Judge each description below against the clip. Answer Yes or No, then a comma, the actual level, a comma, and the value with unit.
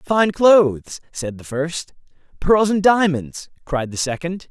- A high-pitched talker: No, medium, 165 Hz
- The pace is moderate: Yes, average, 145 wpm